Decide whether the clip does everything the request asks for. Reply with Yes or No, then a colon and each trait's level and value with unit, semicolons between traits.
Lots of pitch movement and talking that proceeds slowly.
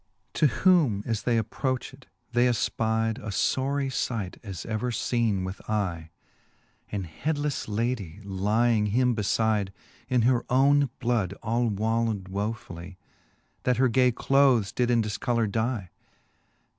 No: average, 3.4 semitones; slow, 130 wpm